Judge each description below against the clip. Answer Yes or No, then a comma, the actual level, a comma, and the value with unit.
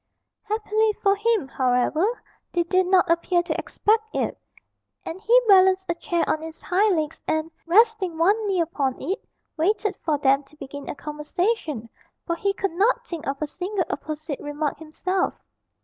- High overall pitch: Yes, very high, 345 Hz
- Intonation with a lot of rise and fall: No, average, 4.6 semitones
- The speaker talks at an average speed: Yes, average, 165 wpm